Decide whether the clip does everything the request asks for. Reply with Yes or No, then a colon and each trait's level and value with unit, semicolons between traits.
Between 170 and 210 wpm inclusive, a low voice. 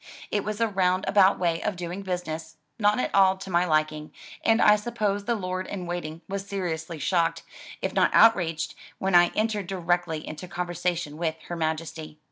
No: average, 180 wpm; medium, 180 Hz